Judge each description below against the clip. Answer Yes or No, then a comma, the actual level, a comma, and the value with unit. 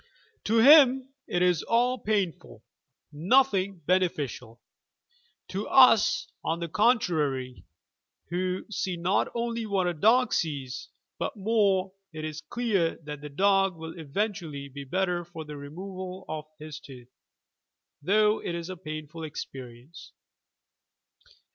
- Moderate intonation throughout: Yes, average, 5.0 semitones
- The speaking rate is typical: No, slow, 130 wpm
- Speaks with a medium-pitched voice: Yes, medium, 180 Hz